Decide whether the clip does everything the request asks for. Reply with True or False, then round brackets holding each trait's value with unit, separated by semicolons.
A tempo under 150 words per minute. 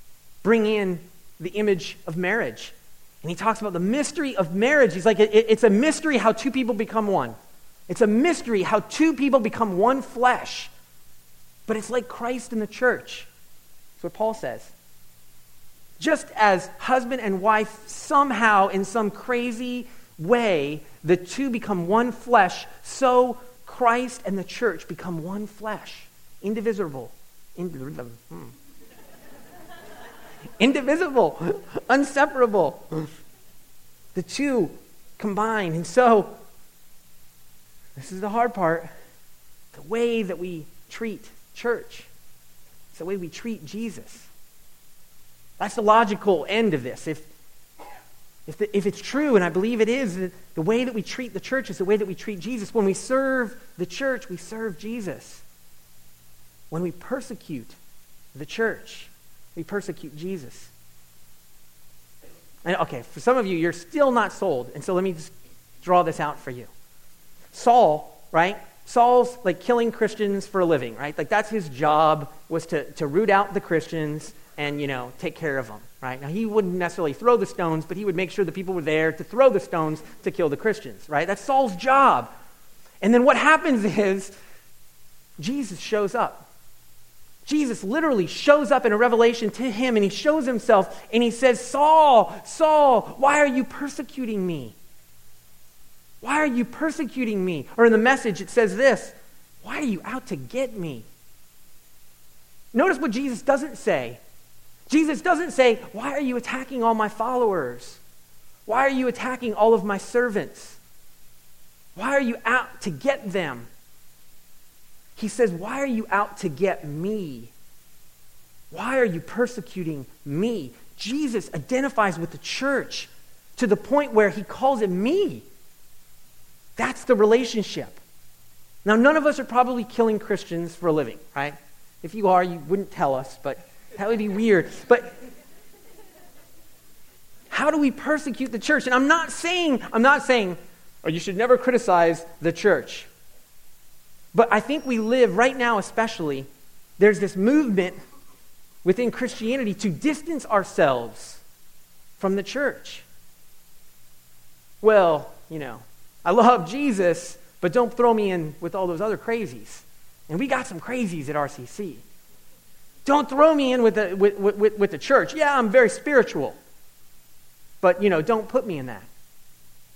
False (155 wpm)